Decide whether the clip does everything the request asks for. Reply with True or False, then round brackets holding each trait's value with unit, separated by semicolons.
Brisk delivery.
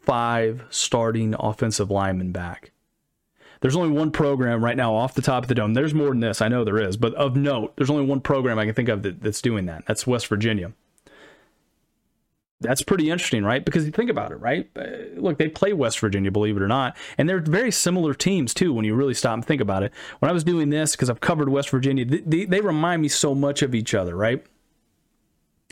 True (225 wpm)